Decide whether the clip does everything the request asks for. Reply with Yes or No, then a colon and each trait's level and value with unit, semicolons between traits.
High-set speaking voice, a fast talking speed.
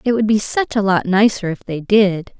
Yes: high, 200 Hz; fast, 250 wpm